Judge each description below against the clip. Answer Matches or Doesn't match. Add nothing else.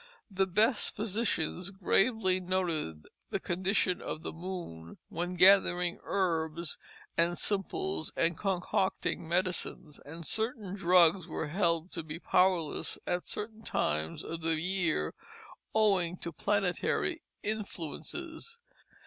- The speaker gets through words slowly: Matches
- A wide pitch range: Doesn't match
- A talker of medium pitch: Matches